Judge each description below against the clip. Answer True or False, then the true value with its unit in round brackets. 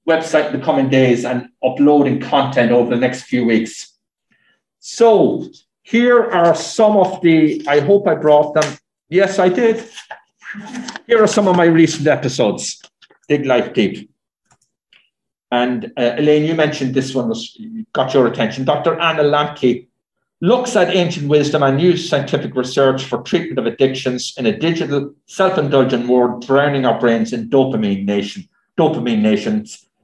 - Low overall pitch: False (150 Hz)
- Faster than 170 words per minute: False (150 wpm)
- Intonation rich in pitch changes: True (5.9 semitones)